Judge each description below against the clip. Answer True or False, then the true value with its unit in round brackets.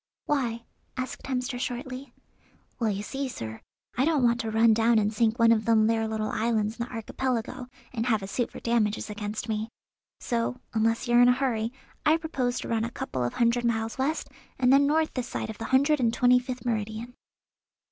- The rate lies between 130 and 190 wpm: False (205 wpm)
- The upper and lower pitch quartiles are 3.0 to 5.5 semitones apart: False (2.4 semitones)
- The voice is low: False (235 Hz)